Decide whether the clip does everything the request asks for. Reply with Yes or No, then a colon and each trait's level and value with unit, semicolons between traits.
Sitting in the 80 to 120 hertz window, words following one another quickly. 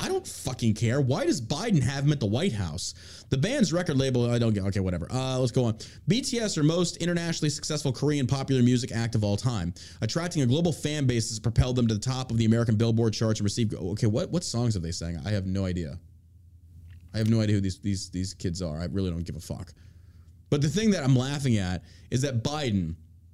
Yes: low, 115 Hz; fast, 240 wpm